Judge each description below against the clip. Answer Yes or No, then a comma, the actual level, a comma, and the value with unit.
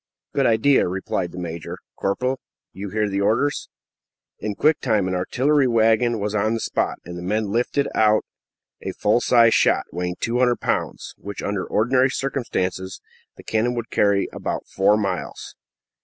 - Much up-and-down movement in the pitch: No, average, 3.9 semitones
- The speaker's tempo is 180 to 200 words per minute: No, average, 165 wpm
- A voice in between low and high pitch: No, low, 110 Hz